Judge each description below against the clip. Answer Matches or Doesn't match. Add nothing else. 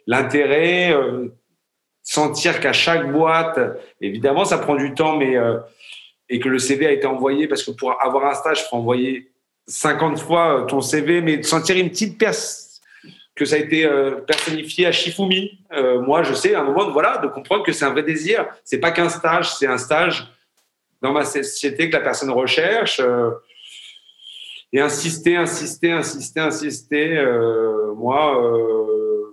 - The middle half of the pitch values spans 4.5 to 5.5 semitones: Doesn't match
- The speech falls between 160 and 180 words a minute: Matches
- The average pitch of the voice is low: Doesn't match